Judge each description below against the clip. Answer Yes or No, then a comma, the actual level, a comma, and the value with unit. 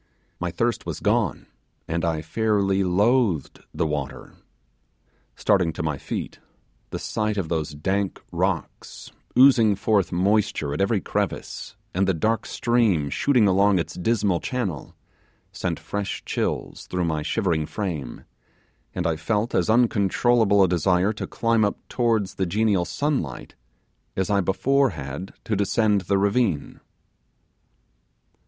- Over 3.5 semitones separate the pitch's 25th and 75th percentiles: Yes, average, 4.5 semitones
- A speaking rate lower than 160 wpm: Yes, slow, 135 wpm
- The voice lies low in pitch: Yes, low, 100 Hz